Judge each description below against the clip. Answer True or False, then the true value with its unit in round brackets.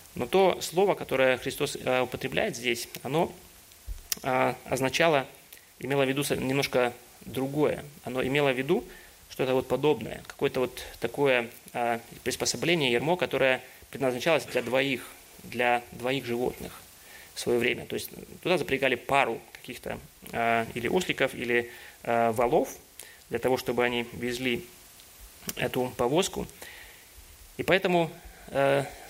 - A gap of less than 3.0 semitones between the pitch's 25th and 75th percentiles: True (2.6 semitones)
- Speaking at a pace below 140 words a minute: True (125 wpm)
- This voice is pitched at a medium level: False (130 Hz)